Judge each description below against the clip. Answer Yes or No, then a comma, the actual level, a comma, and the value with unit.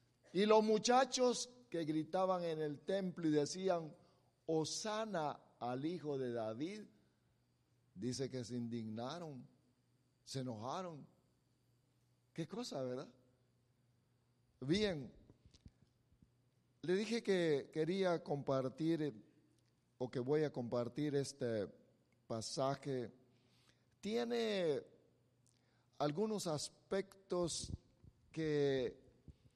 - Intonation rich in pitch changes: Yes, wide, 6.2 semitones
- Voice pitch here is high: No, medium, 140 Hz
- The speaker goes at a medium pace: No, slow, 85 wpm